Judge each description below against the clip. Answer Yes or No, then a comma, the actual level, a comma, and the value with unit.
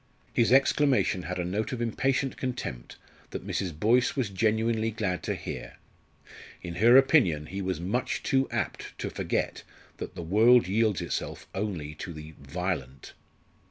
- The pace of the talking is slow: No, average, 155 wpm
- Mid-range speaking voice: No, low, 105 Hz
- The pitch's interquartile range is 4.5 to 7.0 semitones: Yes, wide, 5.6 semitones